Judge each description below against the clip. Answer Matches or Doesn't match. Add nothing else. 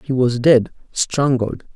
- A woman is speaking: Doesn't match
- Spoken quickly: Doesn't match